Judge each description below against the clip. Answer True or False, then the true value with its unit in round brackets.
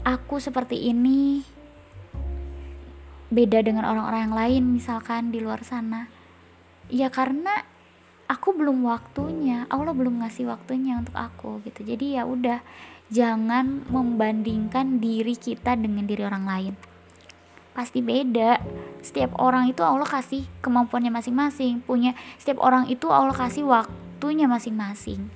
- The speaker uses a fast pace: False (125 wpm)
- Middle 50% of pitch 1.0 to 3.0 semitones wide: True (2.6 semitones)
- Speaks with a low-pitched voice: False (240 Hz)